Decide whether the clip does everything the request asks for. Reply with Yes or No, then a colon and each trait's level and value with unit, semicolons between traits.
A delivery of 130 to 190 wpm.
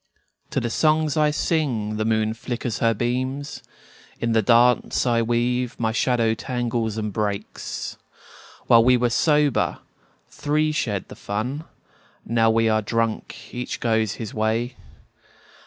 Yes: average, 140 wpm